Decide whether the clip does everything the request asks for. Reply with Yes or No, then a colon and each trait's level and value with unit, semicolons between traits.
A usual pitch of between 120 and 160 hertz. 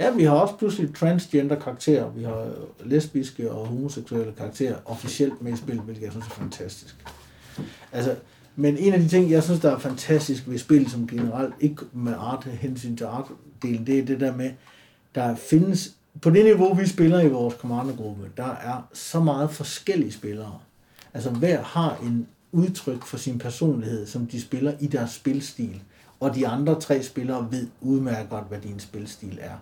Yes: low, 130 Hz